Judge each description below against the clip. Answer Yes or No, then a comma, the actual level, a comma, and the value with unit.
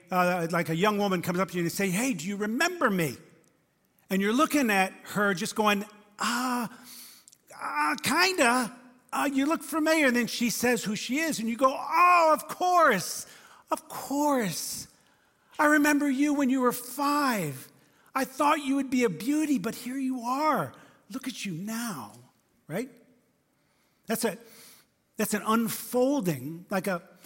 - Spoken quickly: No, average, 170 wpm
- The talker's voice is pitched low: No, high, 235 Hz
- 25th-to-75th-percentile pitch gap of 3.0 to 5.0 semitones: No, wide, 5.5 semitones